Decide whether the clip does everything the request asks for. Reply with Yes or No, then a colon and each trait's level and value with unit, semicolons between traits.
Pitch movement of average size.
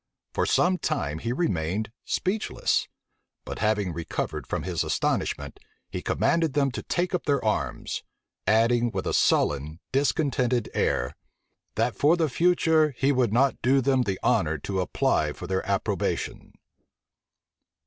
No: wide, 7.4 semitones